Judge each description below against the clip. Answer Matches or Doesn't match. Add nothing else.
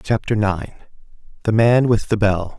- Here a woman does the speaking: Doesn't match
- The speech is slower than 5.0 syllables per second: Matches